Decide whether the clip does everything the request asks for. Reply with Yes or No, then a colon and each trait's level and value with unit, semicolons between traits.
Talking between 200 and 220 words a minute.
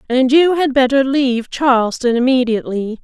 No: average, 140 wpm